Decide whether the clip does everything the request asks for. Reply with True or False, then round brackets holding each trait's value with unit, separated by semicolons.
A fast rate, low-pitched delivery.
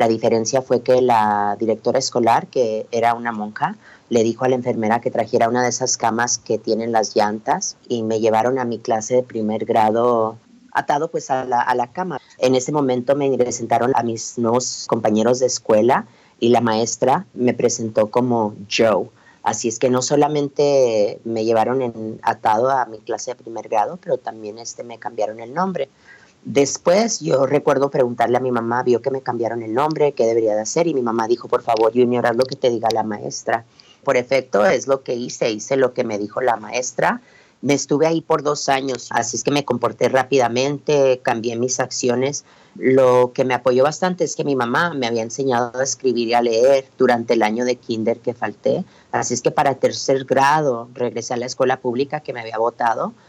True (205 wpm; 125 Hz)